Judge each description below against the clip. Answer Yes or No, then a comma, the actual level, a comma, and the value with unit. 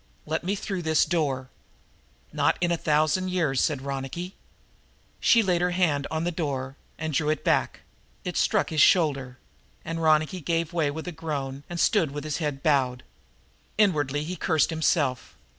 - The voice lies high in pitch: No, medium, 155 Hz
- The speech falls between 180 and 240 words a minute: No, average, 170 wpm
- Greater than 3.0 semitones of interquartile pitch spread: Yes, average, 3.5 semitones